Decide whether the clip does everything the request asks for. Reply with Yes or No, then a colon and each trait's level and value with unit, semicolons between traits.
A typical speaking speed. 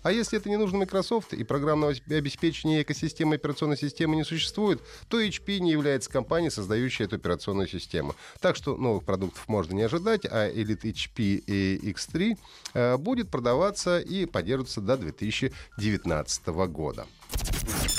Yes: average, 140 wpm